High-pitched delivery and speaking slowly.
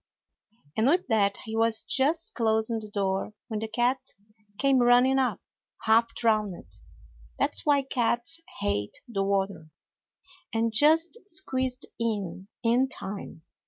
Yes: high, 230 Hz; slow, 125 wpm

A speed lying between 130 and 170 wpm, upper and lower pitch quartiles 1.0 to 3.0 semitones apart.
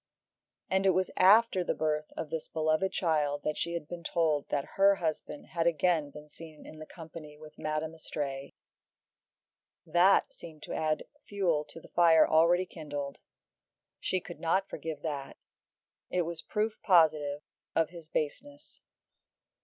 Yes: average, 150 wpm; narrow, 2.5 semitones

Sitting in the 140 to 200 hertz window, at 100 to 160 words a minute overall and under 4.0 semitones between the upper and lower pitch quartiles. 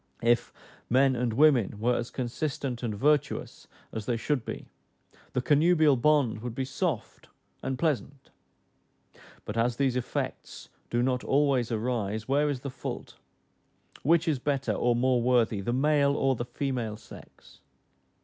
No: low, 125 Hz; average, 150 wpm; average, 3.1 semitones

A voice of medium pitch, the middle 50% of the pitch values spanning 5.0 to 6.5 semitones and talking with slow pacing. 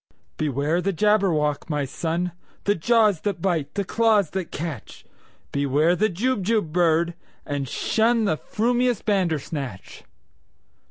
Yes: medium, 175 Hz; wide, 5.4 semitones; slow, 105 wpm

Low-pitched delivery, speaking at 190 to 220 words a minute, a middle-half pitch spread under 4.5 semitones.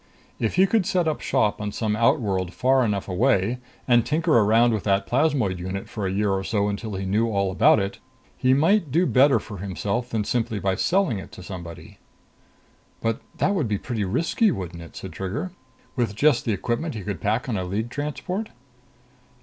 No: low, 110 Hz; average, 200 wpm; wide, 5.6 semitones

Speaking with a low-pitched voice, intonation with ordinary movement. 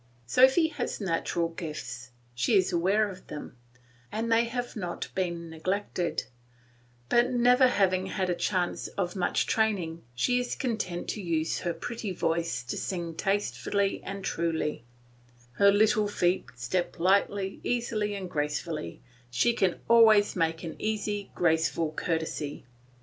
No: medium, 185 Hz; average, 4.3 semitones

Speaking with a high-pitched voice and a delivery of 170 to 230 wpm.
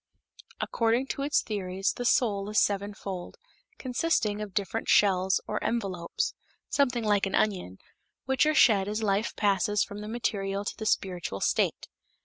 No: high, 205 Hz; average, 150 wpm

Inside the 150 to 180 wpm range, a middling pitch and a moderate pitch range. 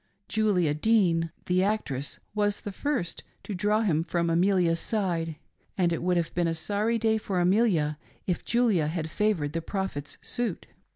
Yes: average, 165 wpm; medium, 180 Hz; average, 4.1 semitones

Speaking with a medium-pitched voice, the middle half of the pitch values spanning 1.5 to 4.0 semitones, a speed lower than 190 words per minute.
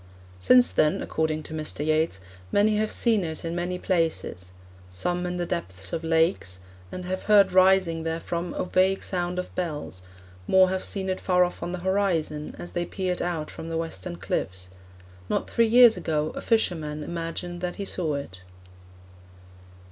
Yes: medium, 175 Hz; average, 3.1 semitones; average, 170 wpm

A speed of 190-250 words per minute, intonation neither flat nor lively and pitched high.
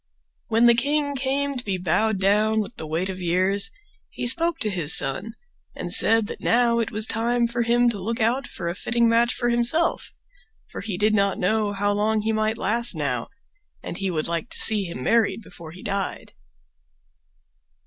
Yes: average, 195 wpm; average, 3.5 semitones; high, 220 Hz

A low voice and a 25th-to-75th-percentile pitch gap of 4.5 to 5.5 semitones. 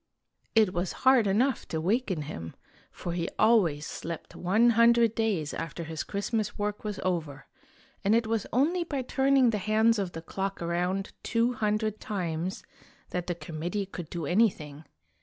No: high, 200 Hz; average, 5.0 semitones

